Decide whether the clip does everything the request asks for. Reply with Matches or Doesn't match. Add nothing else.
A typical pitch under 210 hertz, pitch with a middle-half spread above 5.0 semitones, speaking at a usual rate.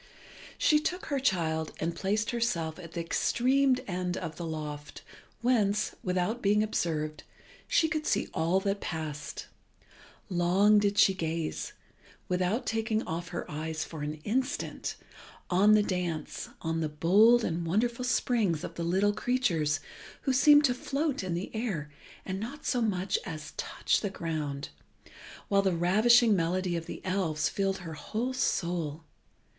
Matches